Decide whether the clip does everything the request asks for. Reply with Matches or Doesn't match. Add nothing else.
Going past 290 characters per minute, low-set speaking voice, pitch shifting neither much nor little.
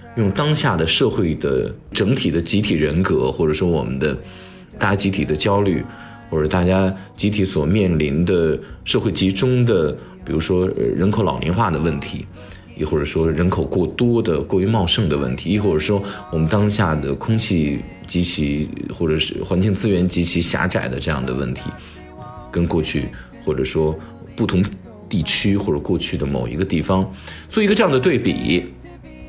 Doesn't match